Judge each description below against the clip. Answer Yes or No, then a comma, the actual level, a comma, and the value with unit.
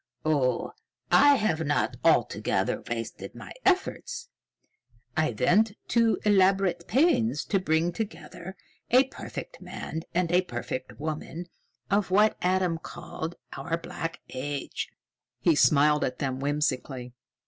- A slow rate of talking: Yes, slow, 120 wpm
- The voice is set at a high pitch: No, medium, 170 Hz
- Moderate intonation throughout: No, wide, 5.7 semitones